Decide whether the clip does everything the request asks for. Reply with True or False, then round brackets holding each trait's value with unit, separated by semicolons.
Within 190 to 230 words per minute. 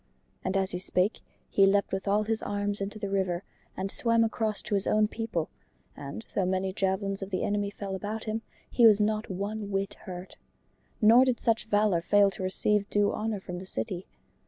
True (200 wpm)